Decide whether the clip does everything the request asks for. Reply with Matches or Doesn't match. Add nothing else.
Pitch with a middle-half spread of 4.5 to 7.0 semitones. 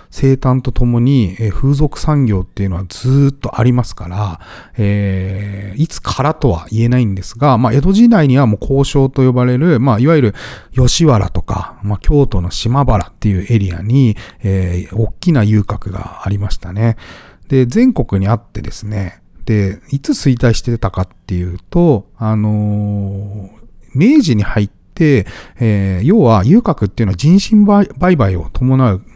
Matches